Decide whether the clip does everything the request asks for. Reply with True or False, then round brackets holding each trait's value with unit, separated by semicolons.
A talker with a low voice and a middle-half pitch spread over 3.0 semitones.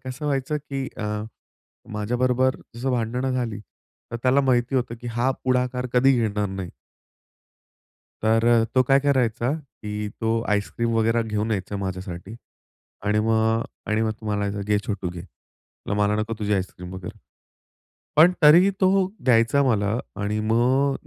True (115 Hz; 3.5 semitones)